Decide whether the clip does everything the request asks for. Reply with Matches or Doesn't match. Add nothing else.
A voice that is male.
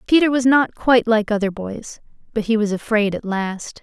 Doesn't match